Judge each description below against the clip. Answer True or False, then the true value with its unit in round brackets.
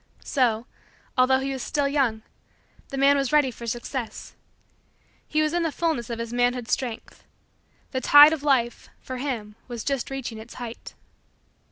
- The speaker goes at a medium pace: True (165 wpm)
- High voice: True (255 Hz)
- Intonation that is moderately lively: True (3.0 semitones)